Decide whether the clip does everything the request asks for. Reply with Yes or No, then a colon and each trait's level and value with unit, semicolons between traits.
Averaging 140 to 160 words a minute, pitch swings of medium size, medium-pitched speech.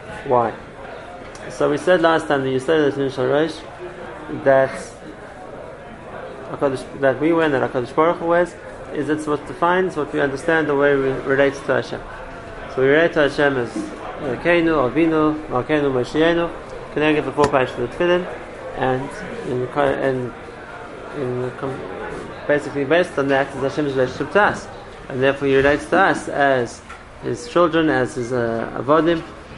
Yes: average, 150 wpm; average, 3.1 semitones; medium, 145 Hz